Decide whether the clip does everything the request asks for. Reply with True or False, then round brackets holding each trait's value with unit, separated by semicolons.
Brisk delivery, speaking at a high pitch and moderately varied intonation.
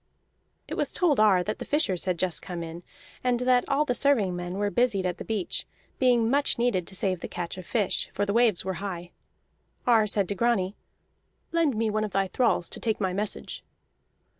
True (210 wpm; 205 Hz; 4.6 semitones)